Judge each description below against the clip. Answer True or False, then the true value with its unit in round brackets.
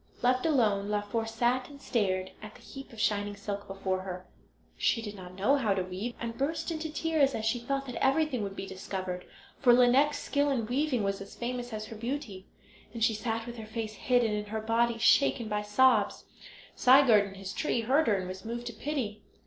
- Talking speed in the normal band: False (210 wpm)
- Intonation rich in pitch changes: False (3.8 semitones)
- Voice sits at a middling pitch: False (225 Hz)